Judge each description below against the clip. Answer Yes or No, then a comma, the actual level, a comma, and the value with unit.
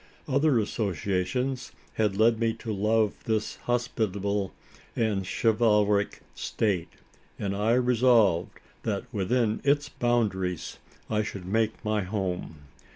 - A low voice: Yes, low, 110 Hz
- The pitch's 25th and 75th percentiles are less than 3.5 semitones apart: Yes, average, 2.9 semitones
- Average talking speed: No, slow, 110 wpm